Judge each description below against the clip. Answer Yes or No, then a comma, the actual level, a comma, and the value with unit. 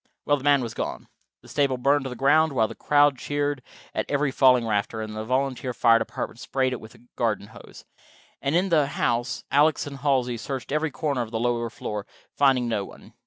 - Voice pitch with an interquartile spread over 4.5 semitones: No, average, 3.6 semitones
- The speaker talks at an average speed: No, fast, 215 wpm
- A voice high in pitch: No, low, 130 Hz